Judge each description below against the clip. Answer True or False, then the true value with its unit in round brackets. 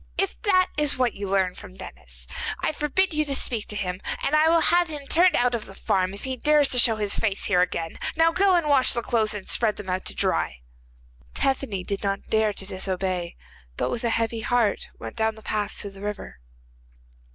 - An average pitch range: False (6.6 semitones)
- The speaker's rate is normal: False (220 wpm)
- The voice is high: True (220 Hz)